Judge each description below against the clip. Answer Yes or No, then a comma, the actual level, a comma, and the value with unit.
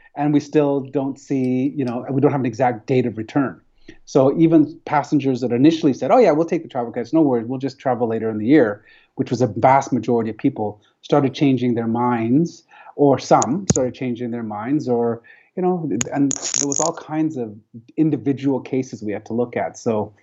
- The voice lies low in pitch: Yes, low, 130 Hz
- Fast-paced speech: Yes, fast, 210 wpm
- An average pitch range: Yes, average, 3.4 semitones